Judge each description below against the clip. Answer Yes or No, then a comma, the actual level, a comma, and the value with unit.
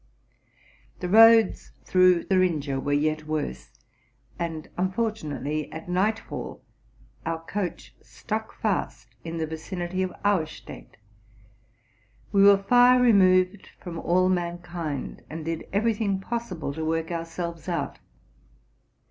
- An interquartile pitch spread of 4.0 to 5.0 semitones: No, average, 3.5 semitones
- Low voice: No, medium, 175 Hz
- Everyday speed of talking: No, slow, 120 wpm